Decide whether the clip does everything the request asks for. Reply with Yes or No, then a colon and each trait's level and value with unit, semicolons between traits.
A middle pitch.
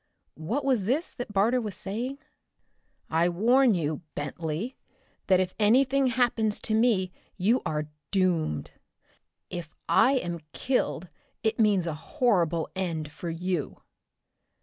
No: high, 195 Hz